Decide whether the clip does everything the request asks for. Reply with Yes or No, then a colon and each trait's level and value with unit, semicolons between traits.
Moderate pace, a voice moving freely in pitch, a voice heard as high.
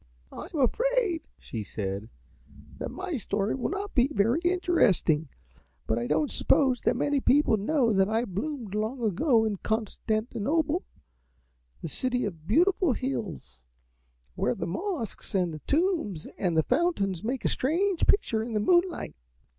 Yes: average, 150 wpm; wide, 8.4 semitones; high, 240 Hz